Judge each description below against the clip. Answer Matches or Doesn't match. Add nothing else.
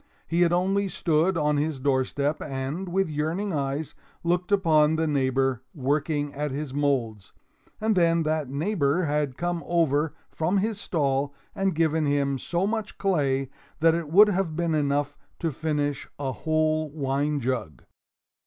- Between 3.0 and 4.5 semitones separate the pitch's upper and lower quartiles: Matches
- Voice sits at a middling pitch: Matches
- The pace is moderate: Matches